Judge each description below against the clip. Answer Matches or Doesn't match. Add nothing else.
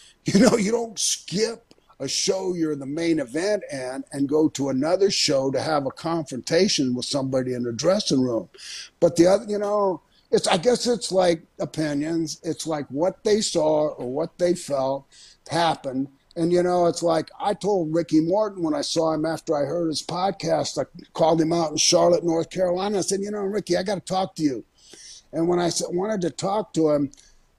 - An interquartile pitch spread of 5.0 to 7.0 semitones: Doesn't match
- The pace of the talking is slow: Doesn't match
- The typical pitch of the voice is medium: Matches